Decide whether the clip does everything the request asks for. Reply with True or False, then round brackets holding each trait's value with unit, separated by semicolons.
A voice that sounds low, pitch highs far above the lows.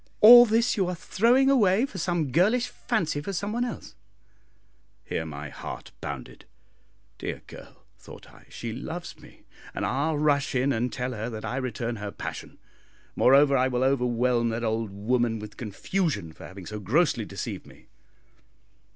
True (130 Hz; 7.9 semitones)